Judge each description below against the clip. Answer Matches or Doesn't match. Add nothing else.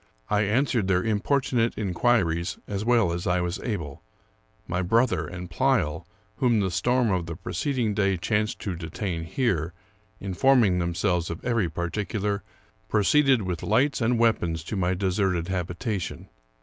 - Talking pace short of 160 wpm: Matches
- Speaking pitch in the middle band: Doesn't match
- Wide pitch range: Doesn't match